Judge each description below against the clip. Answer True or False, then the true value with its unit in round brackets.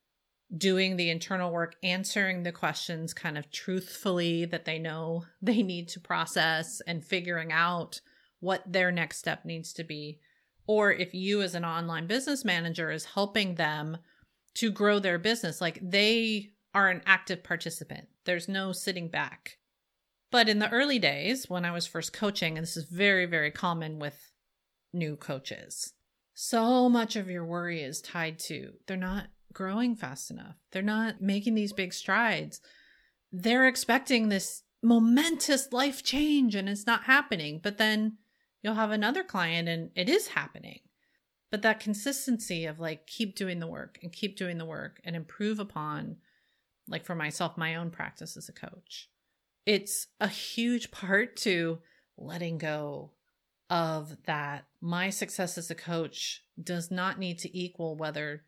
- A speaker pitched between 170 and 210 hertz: True (185 Hz)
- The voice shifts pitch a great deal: False (4.2 semitones)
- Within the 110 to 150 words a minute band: False (160 wpm)